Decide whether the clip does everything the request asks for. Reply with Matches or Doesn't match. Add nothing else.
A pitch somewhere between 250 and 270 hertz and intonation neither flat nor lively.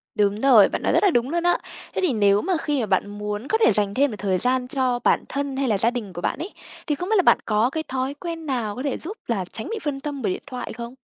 Doesn't match